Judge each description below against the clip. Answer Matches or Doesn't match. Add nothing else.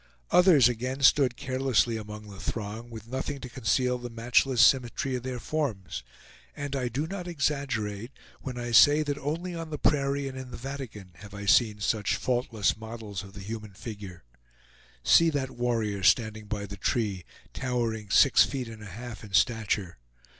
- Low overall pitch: Matches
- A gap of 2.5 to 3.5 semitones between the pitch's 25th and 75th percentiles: Doesn't match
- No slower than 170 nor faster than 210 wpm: Matches